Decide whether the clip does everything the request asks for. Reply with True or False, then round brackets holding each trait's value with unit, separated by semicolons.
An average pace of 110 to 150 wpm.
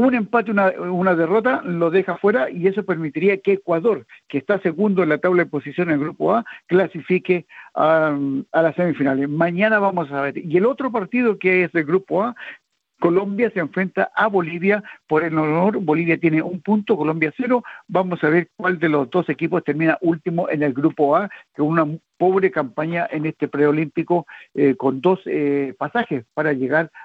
False (185 wpm)